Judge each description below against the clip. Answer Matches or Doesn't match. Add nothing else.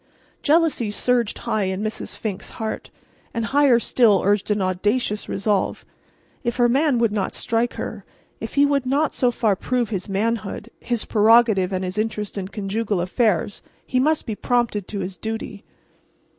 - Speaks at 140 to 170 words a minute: Matches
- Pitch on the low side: Doesn't match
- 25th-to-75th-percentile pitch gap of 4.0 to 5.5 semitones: Doesn't match